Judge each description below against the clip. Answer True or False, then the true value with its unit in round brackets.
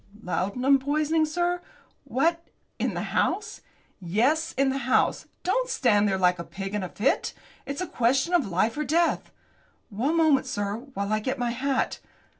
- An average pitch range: False (7.2 semitones)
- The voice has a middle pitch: False (265 Hz)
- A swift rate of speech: False (170 wpm)